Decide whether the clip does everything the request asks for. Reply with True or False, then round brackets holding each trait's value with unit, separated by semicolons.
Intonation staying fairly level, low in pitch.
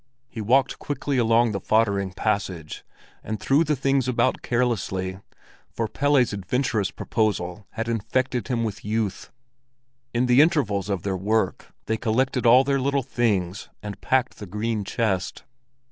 False (4.1 semitones; 115 Hz)